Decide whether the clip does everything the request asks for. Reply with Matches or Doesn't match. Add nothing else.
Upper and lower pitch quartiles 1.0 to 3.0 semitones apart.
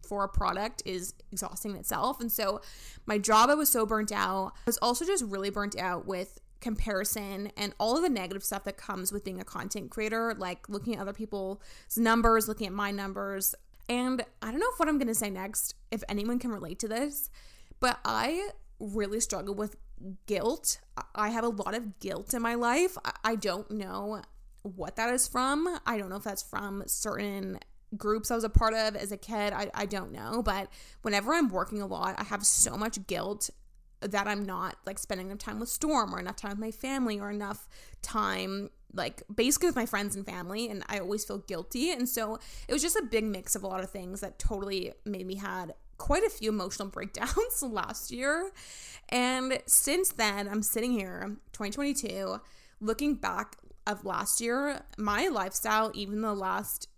Matches